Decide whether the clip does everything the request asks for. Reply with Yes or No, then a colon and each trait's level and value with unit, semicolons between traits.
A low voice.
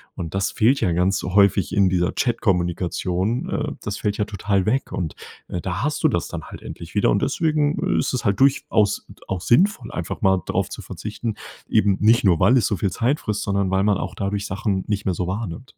Yes: low, 100 Hz